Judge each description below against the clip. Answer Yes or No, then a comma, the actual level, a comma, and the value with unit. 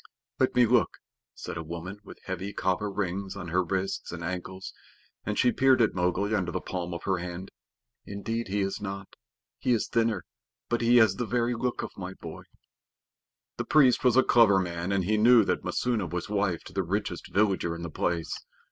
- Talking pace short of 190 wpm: No, average, 200 wpm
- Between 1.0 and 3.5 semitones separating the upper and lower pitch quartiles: No, average, 4.0 semitones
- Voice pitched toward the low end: Yes, low, 100 Hz